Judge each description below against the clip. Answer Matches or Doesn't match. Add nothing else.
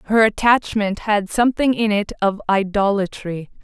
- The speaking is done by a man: Doesn't match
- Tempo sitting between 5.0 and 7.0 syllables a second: Doesn't match